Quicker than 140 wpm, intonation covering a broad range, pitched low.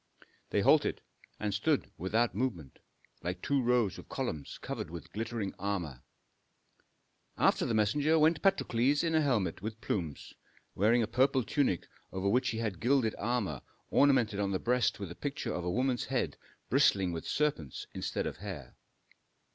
Yes: average, 160 wpm; wide, 5.7 semitones; low, 110 Hz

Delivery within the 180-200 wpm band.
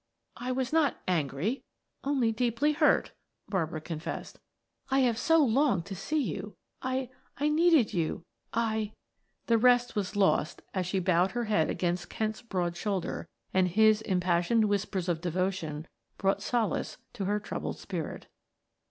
No: average, 150 wpm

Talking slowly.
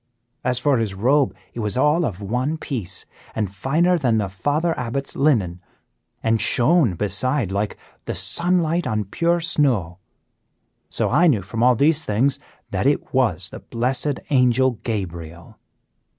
No: average, 150 wpm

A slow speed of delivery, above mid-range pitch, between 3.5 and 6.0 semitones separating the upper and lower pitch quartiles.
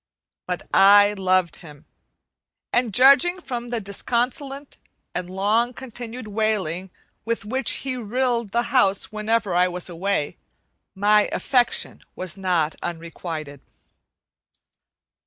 Yes: slow, 110 wpm; high, 210 Hz; average, 4.7 semitones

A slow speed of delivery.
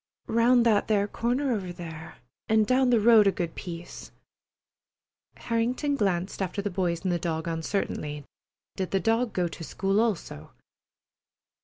No: average, 150 wpm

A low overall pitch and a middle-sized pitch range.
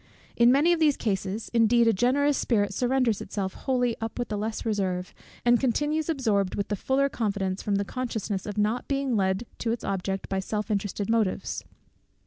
No: high, 225 Hz; average, 3.9 semitones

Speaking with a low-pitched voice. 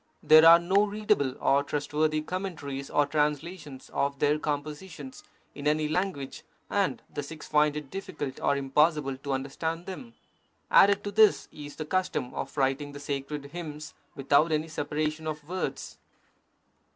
No: medium, 150 Hz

